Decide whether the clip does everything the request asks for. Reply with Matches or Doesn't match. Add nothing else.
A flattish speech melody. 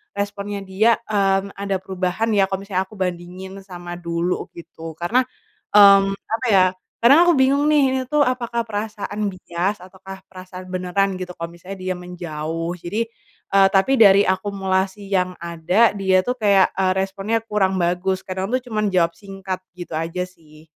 Matches